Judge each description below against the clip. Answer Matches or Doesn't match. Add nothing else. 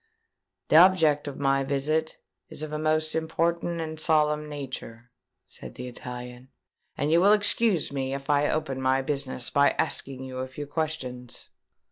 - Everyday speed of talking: Matches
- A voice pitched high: Doesn't match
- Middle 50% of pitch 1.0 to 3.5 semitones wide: Matches